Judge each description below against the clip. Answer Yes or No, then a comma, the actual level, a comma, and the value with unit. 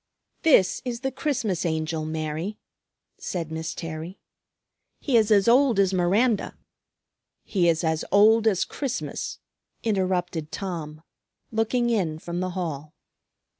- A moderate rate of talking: No, slow, 130 wpm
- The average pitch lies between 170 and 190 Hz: Yes, medium, 185 Hz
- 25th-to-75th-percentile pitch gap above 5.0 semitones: Yes, wide, 5.6 semitones